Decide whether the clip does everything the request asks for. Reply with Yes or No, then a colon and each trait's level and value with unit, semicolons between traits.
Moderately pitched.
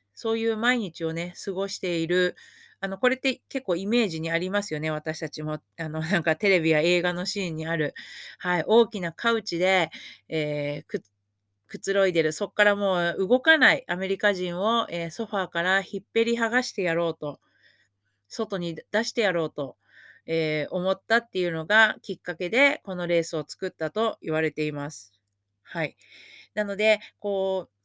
Yes: medium, 180 Hz